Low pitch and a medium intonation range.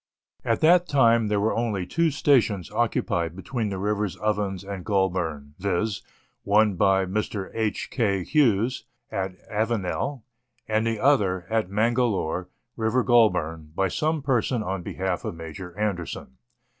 Yes: low, 105 Hz; average, 3.7 semitones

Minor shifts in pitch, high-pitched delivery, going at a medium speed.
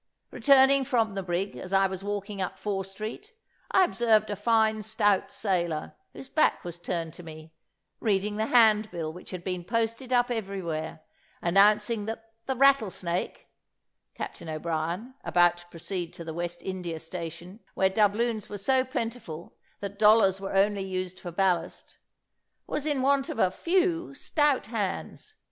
No: average, 4.5 semitones; high, 200 Hz; average, 155 wpm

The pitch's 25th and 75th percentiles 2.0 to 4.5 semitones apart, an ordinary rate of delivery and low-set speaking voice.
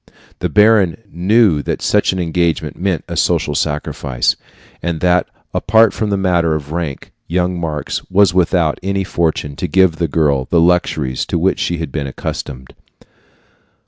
Yes: average, 3.3 semitones; average, 160 wpm; very low, 85 Hz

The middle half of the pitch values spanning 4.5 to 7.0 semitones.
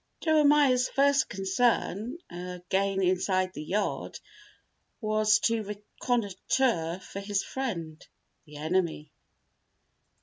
Yes: average, 5.1 semitones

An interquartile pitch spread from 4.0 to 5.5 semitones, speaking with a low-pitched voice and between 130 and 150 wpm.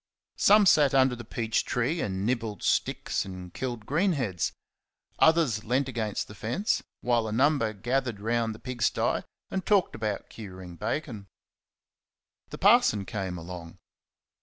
Yes: average, 4.7 semitones; low, 115 Hz; average, 145 wpm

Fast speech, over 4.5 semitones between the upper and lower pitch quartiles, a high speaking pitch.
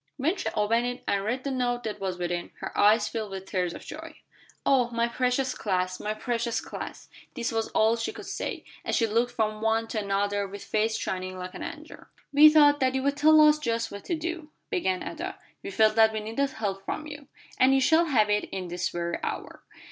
Yes: fast, 215 wpm; average, 5.1 semitones; high, 230 Hz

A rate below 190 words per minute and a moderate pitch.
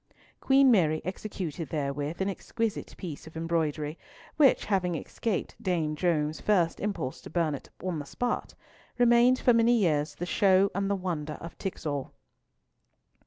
Yes: average, 150 wpm; medium, 175 Hz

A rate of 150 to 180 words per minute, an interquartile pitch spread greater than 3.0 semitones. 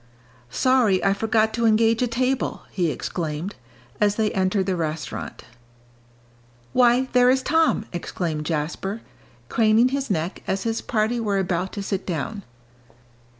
No: average, 140 wpm; average, 4.3 semitones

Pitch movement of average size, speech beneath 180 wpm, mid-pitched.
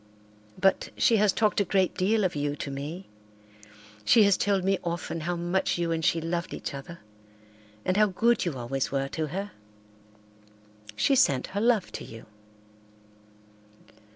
Yes: average, 4.7 semitones; average, 160 wpm; medium, 175 Hz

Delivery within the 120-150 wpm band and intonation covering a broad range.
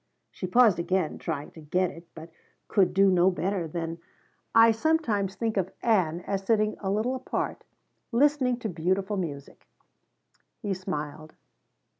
No: average, 145 wpm; average, 4.3 semitones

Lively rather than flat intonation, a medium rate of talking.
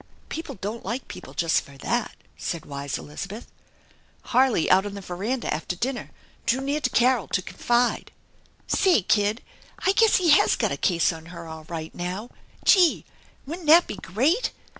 Yes: wide, 7.3 semitones; average, 175 wpm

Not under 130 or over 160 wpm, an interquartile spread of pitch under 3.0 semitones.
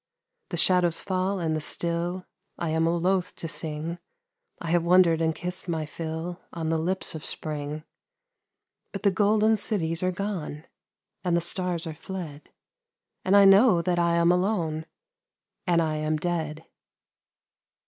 Yes: average, 150 wpm; narrow, 2.4 semitones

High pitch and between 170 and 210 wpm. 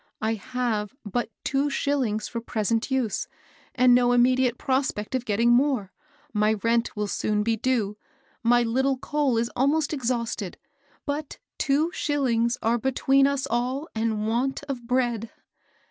No: high, 245 Hz; average, 145 wpm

